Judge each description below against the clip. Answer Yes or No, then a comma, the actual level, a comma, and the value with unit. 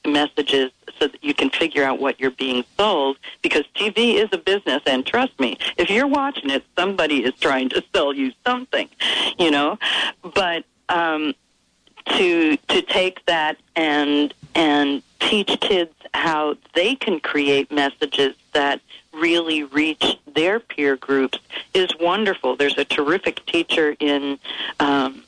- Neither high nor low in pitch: Yes, medium, 150 Hz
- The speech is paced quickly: No, average, 145 wpm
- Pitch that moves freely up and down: Yes, wide, 5.7 semitones